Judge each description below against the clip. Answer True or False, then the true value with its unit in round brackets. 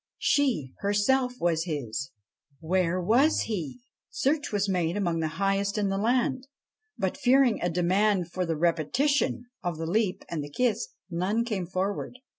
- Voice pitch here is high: True (195 Hz)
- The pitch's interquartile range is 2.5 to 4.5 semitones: False (5.5 semitones)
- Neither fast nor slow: True (155 wpm)